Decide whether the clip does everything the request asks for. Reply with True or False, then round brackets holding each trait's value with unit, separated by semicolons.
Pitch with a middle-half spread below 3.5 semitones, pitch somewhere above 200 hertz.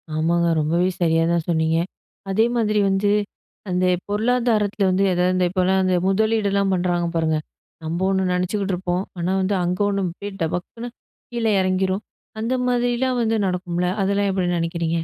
False (2.7 semitones; 185 Hz)